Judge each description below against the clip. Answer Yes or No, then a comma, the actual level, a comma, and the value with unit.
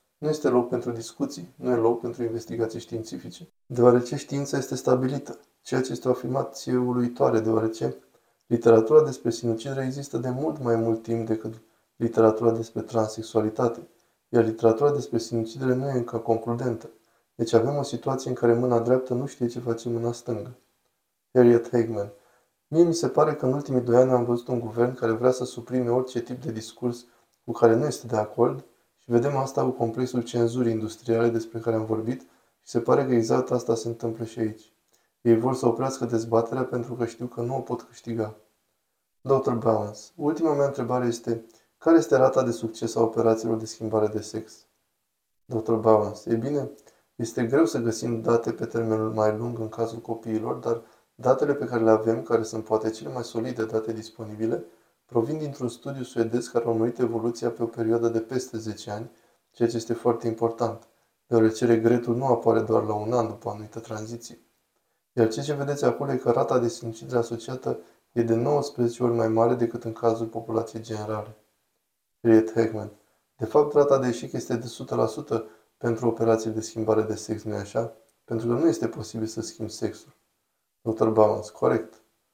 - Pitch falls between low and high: No, low, 115 Hz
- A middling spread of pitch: No, narrow, 1.5 semitones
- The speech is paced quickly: Yes, fast, 180 wpm